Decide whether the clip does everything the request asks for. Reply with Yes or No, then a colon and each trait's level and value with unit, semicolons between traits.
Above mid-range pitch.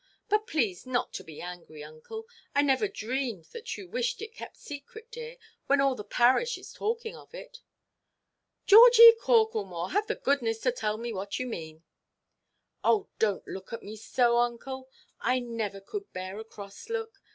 Yes: very high, 255 Hz